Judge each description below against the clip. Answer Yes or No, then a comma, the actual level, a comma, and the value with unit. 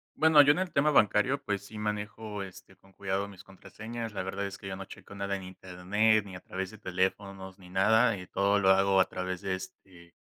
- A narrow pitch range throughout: Yes, narrow, 2.0 semitones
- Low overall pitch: Yes, low, 100 Hz